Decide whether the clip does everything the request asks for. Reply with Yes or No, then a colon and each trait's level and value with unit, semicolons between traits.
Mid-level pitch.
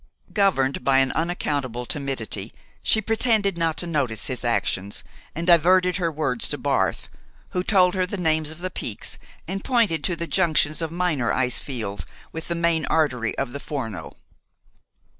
Yes: medium, 160 Hz